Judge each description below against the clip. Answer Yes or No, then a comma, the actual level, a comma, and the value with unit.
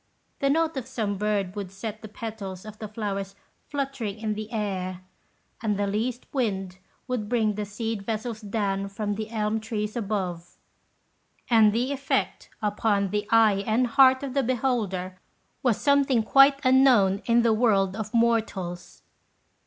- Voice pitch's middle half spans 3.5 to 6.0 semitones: No, average, 3.1 semitones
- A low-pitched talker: No, high, 215 Hz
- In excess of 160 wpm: No, average, 155 wpm